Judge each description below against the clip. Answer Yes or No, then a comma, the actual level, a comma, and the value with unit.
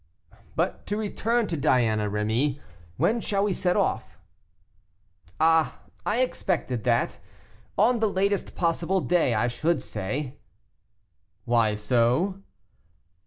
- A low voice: No, medium, 160 Hz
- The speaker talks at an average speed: No, slow, 115 wpm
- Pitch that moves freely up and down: Yes, wide, 8.7 semitones